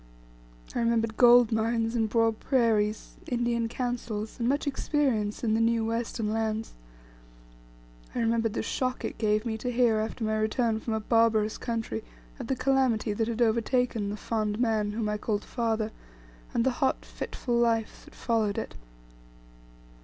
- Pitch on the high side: Yes, high, 225 Hz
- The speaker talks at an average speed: Yes, average, 160 wpm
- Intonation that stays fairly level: Yes, narrow, 1.7 semitones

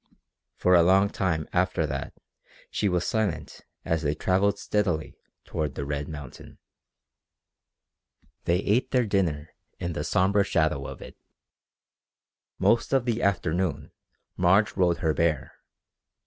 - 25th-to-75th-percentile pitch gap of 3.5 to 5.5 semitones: Yes, average, 4.2 semitones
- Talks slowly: Yes, slow, 130 wpm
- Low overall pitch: Yes, very low, 90 Hz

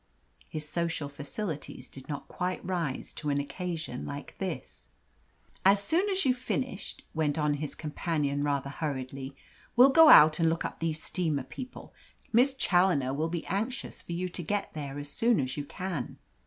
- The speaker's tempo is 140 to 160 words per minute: No, average, 170 wpm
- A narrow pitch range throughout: No, average, 5.0 semitones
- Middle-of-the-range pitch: Yes, medium, 160 Hz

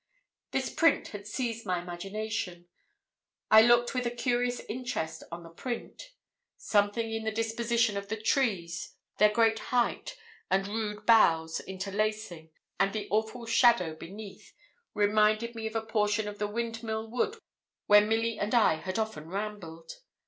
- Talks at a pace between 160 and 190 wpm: No, average, 150 wpm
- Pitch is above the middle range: Yes, high, 215 Hz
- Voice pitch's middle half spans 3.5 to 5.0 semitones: No, average, 2.7 semitones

